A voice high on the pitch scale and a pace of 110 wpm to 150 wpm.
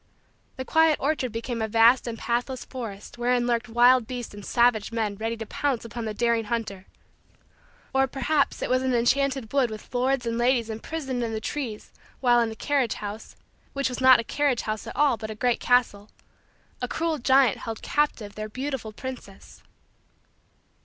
No: high, 240 Hz; average, 180 wpm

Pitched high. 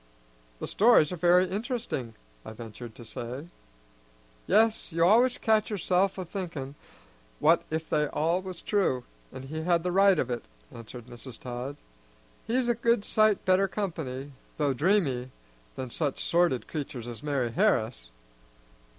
No: medium, 160 Hz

